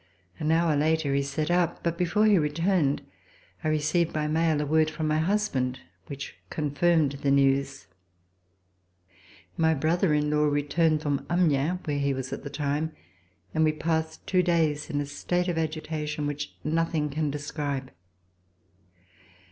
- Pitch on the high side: No, medium, 155 Hz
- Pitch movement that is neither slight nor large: No, narrow, 2.3 semitones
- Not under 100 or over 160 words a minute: Yes, average, 155 wpm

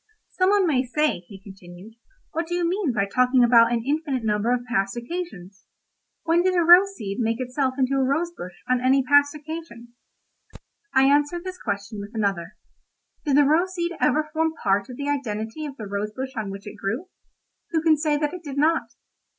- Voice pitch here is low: No, very high, 265 Hz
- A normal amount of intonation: No, wide, 6.4 semitones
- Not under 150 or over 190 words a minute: No, average, 200 wpm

